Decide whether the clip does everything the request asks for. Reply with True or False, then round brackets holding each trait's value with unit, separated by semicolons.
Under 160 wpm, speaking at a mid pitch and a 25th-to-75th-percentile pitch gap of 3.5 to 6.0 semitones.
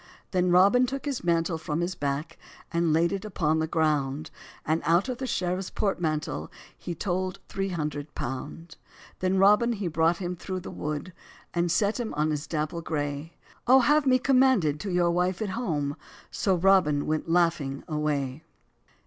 False (170 wpm; 170 Hz; 4.0 semitones)